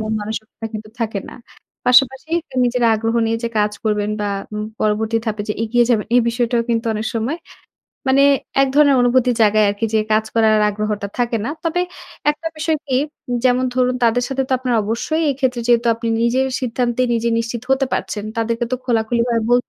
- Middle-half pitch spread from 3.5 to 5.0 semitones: No, narrow, 2.5 semitones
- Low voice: No, high, 235 Hz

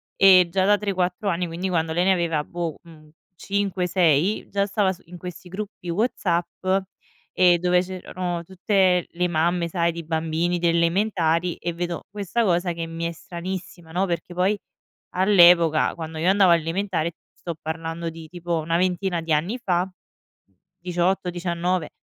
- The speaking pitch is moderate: Yes, medium, 175 Hz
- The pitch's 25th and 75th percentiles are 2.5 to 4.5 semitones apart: No, narrow, 1.9 semitones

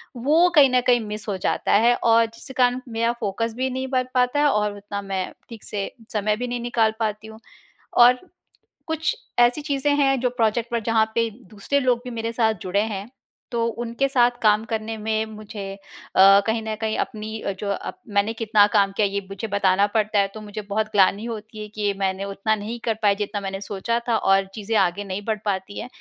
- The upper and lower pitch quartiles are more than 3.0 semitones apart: No, average, 2.7 semitones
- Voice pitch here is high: Yes, high, 220 Hz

